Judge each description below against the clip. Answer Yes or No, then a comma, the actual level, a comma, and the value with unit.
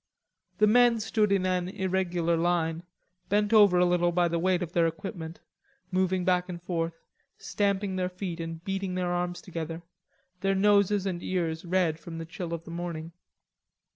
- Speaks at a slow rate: No, average, 170 wpm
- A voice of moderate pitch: Yes, medium, 180 Hz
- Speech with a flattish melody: Yes, narrow, 2.2 semitones